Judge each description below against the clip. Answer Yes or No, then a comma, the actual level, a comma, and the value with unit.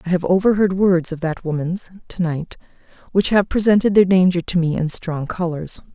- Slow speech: No, average, 190 wpm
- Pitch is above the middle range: No, medium, 180 Hz